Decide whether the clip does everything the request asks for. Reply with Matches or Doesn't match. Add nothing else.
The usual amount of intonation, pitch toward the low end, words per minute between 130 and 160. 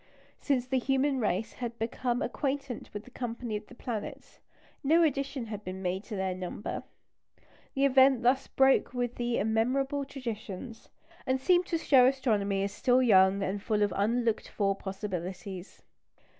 Doesn't match